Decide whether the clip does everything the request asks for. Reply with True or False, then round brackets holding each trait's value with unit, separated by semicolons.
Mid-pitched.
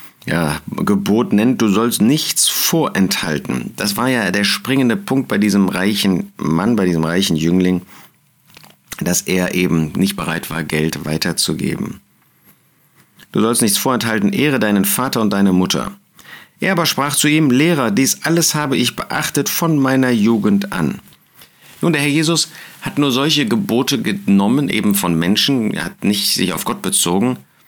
False (105 Hz)